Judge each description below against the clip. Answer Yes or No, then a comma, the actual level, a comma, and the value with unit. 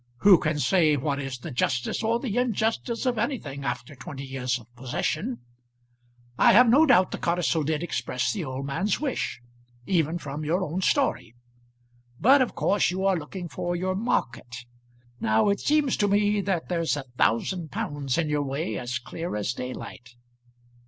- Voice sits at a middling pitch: Yes, medium, 165 Hz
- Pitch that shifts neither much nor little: No, wide, 7.2 semitones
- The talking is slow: No, average, 170 wpm